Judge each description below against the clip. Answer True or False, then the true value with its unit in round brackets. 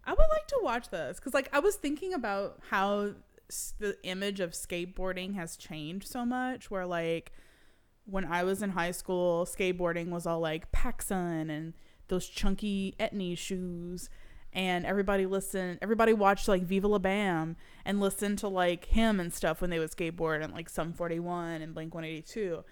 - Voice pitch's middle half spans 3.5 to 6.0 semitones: False (2.9 semitones)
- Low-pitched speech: False (185 Hz)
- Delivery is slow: False (175 wpm)